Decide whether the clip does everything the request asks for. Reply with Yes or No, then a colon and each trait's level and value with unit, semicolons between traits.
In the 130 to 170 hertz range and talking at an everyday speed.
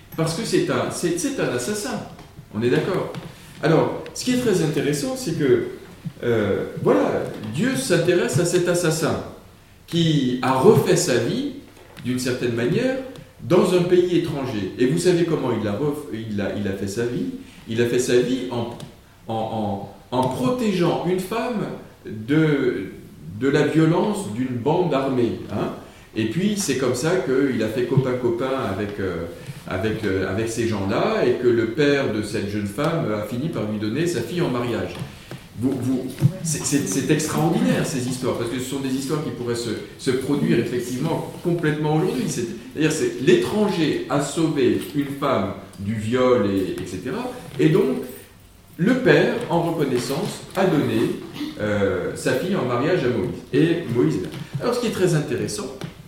Yes: low, 135 Hz; average, 175 wpm